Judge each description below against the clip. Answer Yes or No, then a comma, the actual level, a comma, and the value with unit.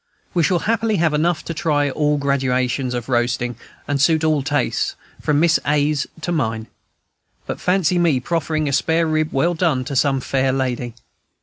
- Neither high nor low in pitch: Yes, medium, 145 Hz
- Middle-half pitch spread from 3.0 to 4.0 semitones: Yes, average, 3.7 semitones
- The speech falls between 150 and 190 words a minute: Yes, average, 175 wpm